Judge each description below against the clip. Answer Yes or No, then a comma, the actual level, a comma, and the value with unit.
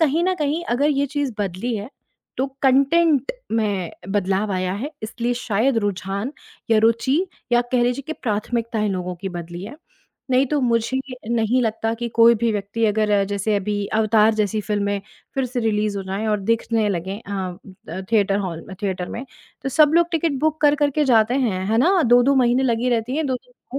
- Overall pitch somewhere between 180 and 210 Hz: No, high, 230 Hz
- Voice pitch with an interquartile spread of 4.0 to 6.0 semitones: Yes, average, 4.4 semitones